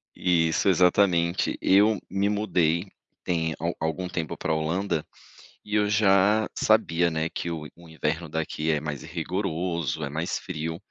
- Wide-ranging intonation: No, average, 3.3 semitones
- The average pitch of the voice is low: Yes, very low, 85 Hz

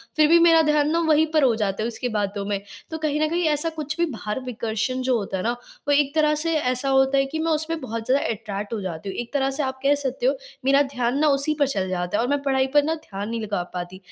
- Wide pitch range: Yes, wide, 5.7 semitones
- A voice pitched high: Yes, very high, 265 Hz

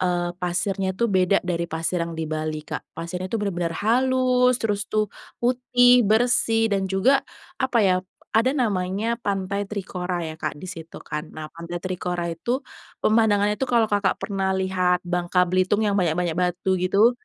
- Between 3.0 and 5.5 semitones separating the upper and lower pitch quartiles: Yes, average, 3.8 semitones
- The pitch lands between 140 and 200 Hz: Yes, high, 190 Hz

